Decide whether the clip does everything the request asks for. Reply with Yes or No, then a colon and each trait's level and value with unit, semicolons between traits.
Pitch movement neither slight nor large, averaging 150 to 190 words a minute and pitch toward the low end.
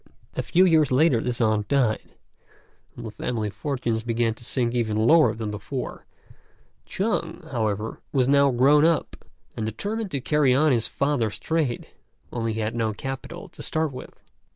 Yes: average, 4.6 semitones; average, 165 wpm; low, 125 Hz